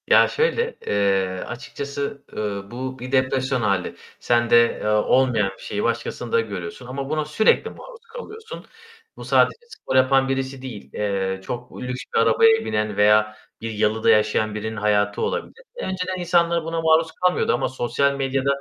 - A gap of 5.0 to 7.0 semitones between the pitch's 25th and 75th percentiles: Yes, wide, 5.6 semitones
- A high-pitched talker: No, low, 125 Hz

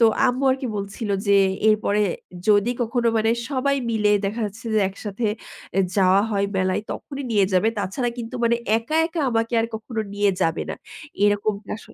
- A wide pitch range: No, average, 2.7 semitones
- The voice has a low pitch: No, high, 215 Hz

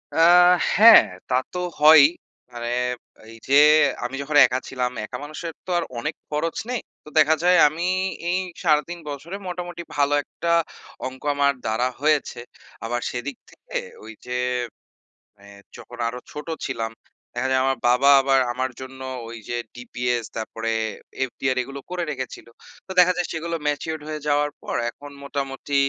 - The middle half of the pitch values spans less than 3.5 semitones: No, average, 4.0 semitones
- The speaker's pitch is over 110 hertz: Yes, medium, 140 Hz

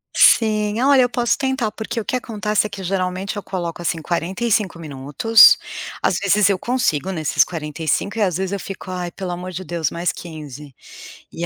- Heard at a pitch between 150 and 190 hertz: Yes, medium, 185 Hz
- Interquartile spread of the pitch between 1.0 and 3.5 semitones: No, average, 3.9 semitones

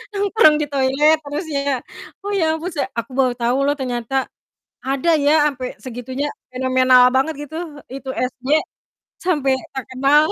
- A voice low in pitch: No, very high, 270 Hz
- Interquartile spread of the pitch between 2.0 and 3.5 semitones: Yes, average, 2.8 semitones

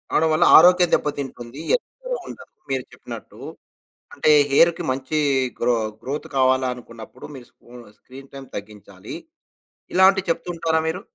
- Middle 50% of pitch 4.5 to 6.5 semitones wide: Yes, average, 4.8 semitones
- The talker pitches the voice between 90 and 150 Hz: Yes, low, 135 Hz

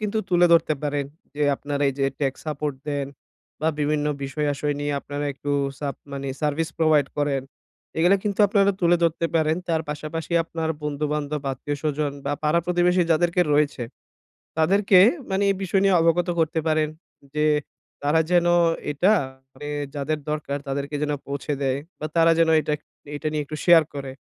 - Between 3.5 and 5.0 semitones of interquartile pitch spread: No, narrow, 2.5 semitones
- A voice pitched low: No, medium, 150 Hz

